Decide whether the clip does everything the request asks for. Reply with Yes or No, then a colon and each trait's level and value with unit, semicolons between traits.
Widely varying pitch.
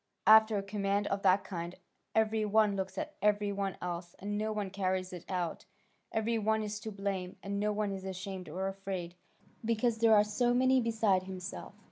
No: narrow, 2.4 semitones